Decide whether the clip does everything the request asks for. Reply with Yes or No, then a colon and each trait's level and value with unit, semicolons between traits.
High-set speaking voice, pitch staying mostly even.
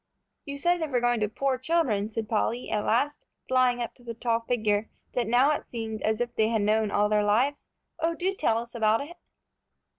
No: high, 235 Hz; average, 3.8 semitones